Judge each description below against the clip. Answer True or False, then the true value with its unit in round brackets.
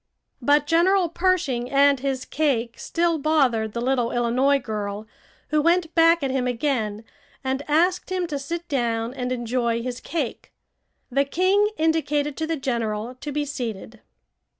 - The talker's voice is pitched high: True (275 Hz)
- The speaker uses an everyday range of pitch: True (5.0 semitones)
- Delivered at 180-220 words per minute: False (150 wpm)